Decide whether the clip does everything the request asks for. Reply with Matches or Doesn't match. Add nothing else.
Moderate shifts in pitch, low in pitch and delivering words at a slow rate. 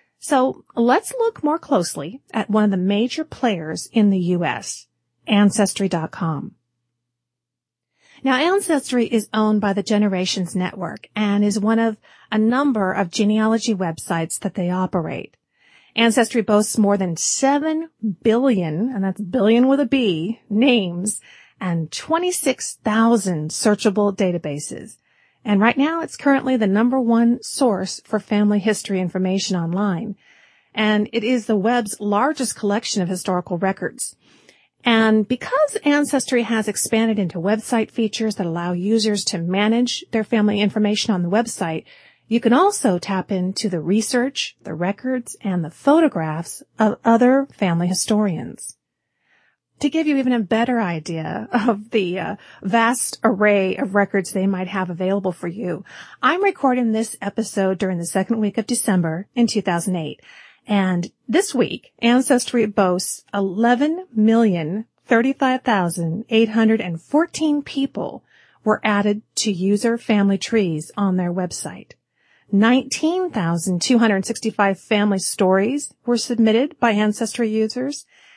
Doesn't match